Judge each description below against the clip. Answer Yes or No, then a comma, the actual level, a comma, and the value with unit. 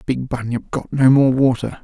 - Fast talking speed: No, average, 195 wpm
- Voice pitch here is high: No, low, 130 Hz